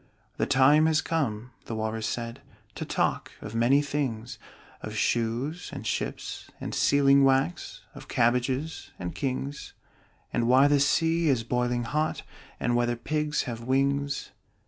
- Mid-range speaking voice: No, low, 130 Hz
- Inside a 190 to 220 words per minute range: No, average, 145 wpm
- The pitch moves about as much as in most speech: Yes, average, 3.4 semitones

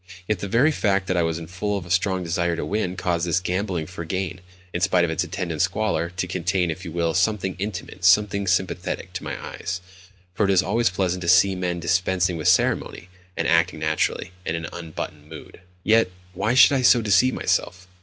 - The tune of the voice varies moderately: No, narrow, 2.3 semitones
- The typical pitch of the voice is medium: No, very low, 90 Hz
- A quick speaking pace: Yes, fast, 210 wpm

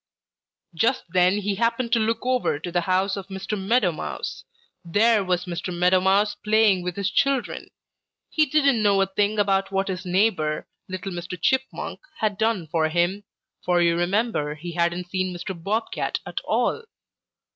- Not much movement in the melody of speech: No, average, 3.4 semitones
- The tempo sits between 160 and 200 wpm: Yes, average, 170 wpm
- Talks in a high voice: Yes, high, 195 Hz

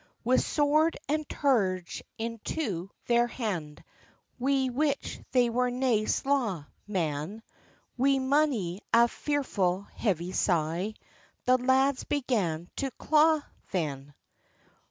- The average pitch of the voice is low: No, high, 235 Hz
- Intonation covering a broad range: Yes, wide, 6.8 semitones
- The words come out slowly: Yes, slow, 105 wpm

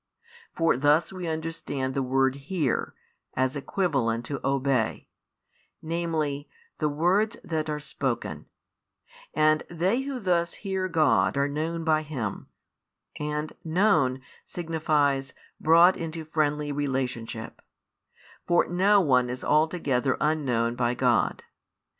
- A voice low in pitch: No, medium, 150 Hz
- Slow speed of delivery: Yes, slow, 115 wpm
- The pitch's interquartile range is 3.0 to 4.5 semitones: Yes, average, 3.8 semitones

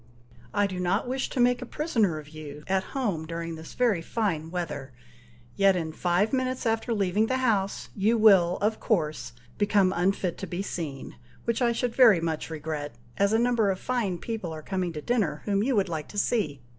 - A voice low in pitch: No, high, 195 Hz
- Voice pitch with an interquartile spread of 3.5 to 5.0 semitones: No, wide, 5.4 semitones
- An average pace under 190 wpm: No, average, 200 wpm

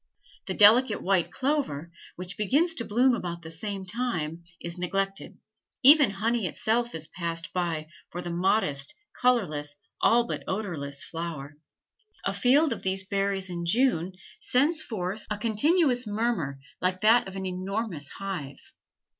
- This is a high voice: Yes, high, 195 Hz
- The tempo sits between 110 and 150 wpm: Yes, average, 145 wpm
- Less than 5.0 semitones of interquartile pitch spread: No, wide, 5.4 semitones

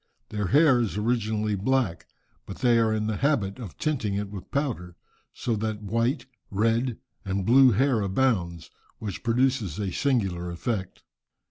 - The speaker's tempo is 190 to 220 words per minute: No, average, 150 wpm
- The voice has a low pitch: Yes, low, 110 Hz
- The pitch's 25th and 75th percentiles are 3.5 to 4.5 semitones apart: Yes, average, 4.1 semitones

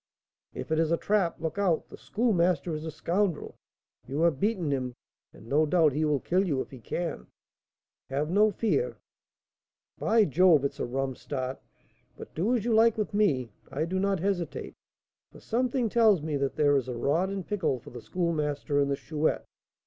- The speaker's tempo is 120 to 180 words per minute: No, average, 195 wpm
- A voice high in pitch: No, medium, 165 Hz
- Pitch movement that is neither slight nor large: No, wide, 5.8 semitones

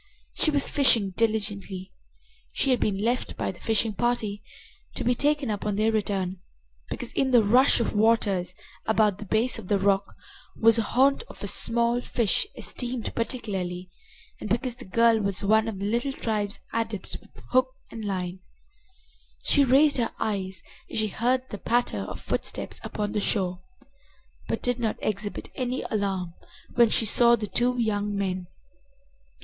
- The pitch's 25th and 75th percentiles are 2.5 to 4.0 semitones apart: Yes, average, 3.2 semitones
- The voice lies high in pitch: Yes, high, 220 Hz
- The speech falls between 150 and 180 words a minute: Yes, average, 165 wpm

